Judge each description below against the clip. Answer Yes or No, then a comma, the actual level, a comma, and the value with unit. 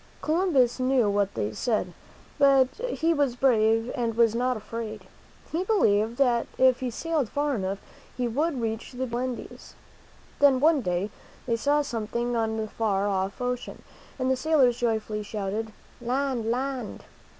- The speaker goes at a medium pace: Yes, average, 155 wpm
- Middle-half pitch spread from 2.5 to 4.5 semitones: Yes, average, 3.5 semitones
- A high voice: Yes, high, 240 Hz